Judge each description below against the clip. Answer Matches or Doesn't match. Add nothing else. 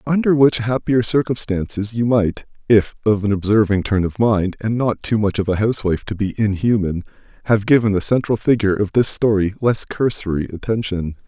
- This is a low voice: Matches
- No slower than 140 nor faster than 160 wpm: Doesn't match